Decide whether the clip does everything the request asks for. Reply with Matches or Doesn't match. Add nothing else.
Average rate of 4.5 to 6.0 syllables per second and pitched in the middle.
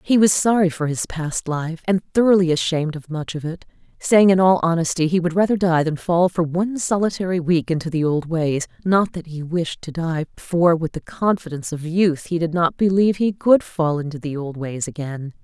Matches